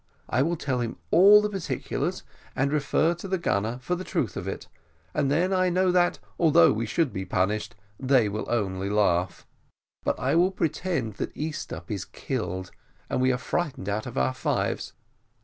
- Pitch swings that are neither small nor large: No, wide, 8.7 semitones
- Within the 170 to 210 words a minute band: Yes, average, 185 wpm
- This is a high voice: No, low, 130 Hz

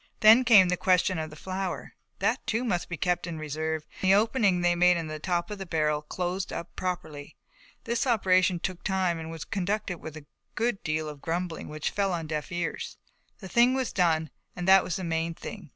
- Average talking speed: No, fast, 215 wpm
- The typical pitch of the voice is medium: Yes, medium, 180 Hz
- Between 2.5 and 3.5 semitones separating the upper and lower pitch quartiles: Yes, average, 3.2 semitones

